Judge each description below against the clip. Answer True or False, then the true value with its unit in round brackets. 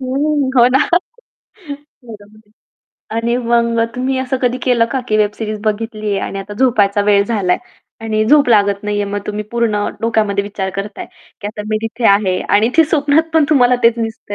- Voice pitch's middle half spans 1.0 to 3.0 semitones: False (3.4 semitones)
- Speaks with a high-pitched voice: True (225 Hz)